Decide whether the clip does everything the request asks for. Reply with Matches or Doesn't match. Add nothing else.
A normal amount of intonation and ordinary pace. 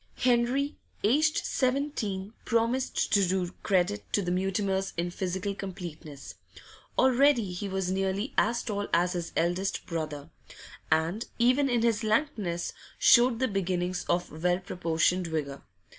Doesn't match